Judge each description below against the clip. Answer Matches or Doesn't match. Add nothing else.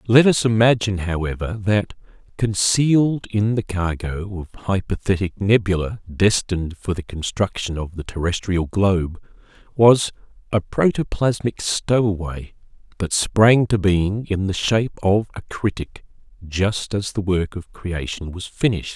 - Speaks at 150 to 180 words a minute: Doesn't match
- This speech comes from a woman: Doesn't match